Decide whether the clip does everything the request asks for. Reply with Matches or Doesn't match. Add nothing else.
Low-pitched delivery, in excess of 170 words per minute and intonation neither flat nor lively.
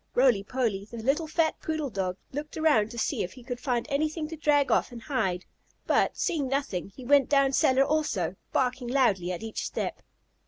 Doesn't match